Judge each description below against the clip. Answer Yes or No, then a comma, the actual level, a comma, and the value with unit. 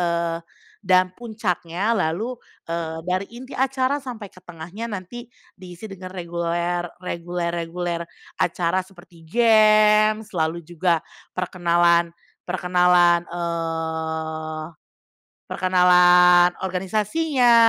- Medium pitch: Yes, medium, 180 Hz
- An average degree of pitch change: Yes, average, 3.1 semitones